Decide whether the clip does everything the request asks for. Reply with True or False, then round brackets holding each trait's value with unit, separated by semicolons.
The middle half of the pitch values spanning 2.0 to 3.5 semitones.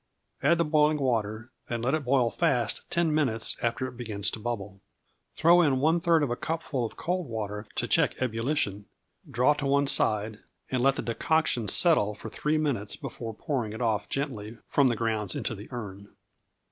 False (5.3 semitones)